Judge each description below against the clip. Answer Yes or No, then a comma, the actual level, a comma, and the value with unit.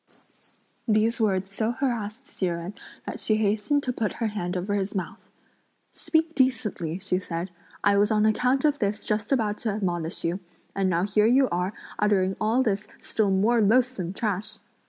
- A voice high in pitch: Yes, high, 210 Hz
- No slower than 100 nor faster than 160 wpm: No, average, 175 wpm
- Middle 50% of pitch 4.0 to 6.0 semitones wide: No, average, 3.3 semitones